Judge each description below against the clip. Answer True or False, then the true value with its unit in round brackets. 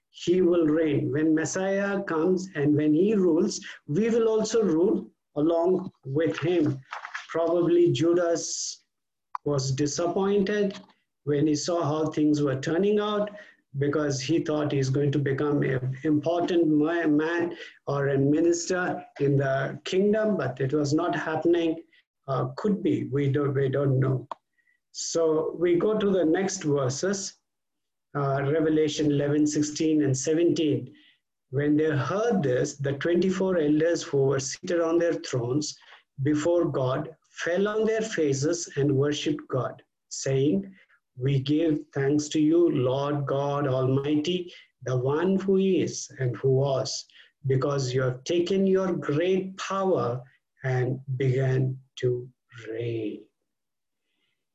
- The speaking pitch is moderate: True (155 Hz)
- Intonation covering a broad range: False (3.7 semitones)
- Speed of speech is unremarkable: False (130 wpm)